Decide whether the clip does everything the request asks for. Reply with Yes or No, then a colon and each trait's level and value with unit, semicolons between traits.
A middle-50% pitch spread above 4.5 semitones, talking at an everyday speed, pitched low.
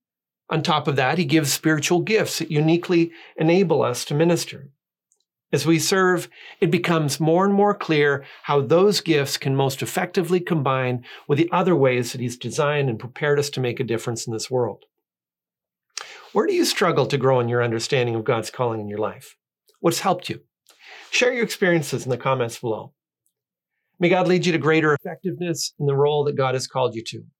No: average, 5.1 semitones; average, 195 wpm; medium, 150 Hz